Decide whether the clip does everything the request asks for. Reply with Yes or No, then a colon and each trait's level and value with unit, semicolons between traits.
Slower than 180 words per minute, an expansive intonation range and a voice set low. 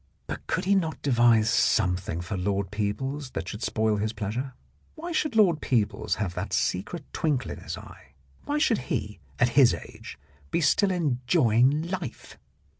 Yes: average, 165 wpm; wide, 7.2 semitones; low, 125 Hz